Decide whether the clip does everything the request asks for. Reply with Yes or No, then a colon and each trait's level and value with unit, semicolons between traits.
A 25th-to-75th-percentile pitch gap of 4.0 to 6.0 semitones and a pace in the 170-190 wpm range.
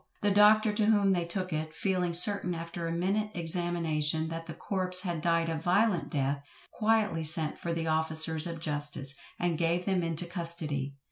No: narrow, 2.5 semitones; average, 180 wpm